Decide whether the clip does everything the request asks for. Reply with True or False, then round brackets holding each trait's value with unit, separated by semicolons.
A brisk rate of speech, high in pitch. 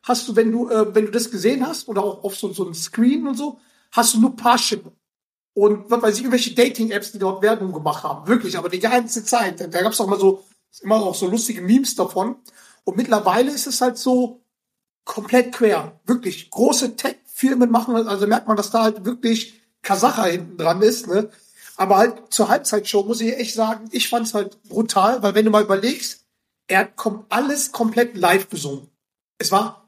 True (205 wpm; 225 Hz)